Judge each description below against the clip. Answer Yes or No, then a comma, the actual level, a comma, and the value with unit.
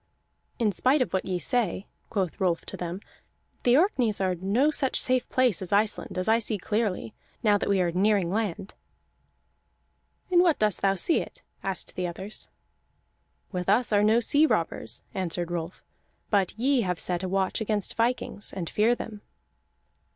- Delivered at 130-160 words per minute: No, average, 170 wpm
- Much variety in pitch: No, average, 4.1 semitones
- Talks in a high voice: Yes, high, 205 Hz